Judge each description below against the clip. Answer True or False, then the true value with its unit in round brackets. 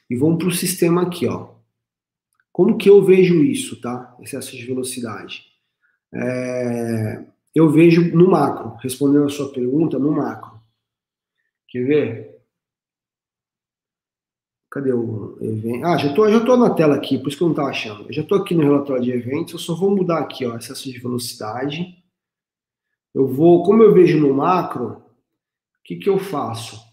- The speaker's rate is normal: True (170 wpm)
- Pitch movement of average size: False (6.1 semitones)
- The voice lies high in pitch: False (140 Hz)